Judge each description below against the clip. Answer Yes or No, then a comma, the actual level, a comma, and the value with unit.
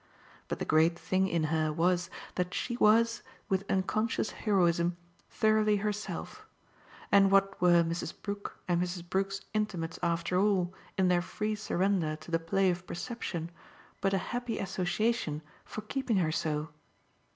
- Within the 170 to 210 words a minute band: No, average, 150 wpm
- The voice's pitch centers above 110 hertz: Yes, medium, 185 Hz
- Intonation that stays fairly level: No, average, 3.5 semitones